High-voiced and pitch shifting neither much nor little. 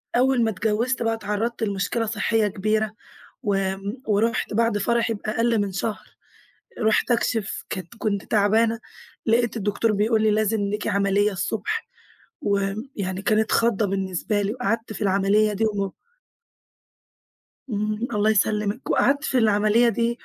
No: high, 215 Hz; narrow, 2.2 semitones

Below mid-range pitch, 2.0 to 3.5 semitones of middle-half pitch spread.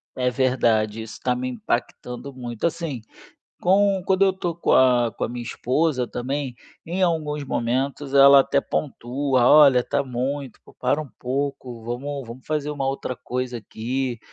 Yes: low, 130 Hz; average, 2.9 semitones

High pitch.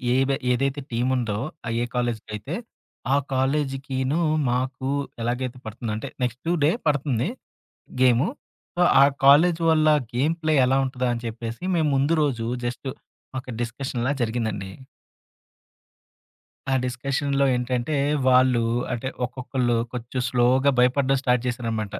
No: low, 130 Hz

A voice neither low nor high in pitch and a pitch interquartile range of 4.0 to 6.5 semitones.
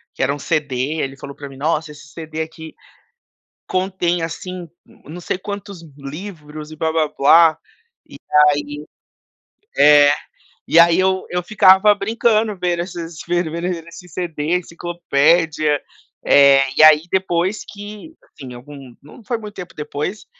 No: medium, 165 Hz; average, 3.6 semitones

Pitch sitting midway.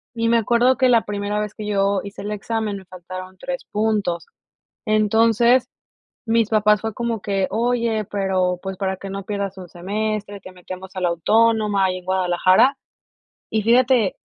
No: high, 205 Hz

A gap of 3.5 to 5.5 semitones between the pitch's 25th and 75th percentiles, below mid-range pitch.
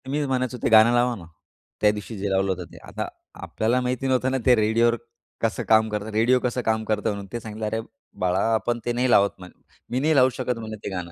No: average, 2.9 semitones; low, 115 Hz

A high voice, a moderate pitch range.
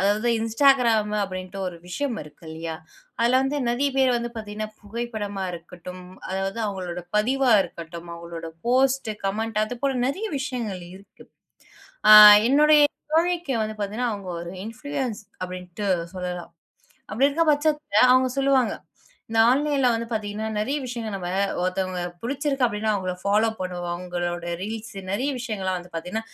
No: high, 215 Hz; wide, 5.7 semitones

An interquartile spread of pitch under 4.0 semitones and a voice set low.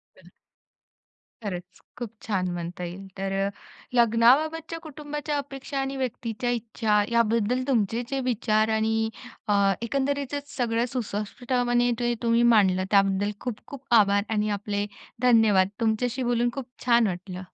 No: average, 3.5 semitones; high, 230 Hz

